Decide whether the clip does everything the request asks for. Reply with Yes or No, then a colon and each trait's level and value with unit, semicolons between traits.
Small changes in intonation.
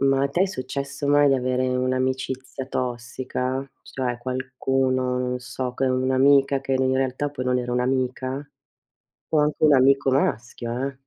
Yes: narrow, 1.2 semitones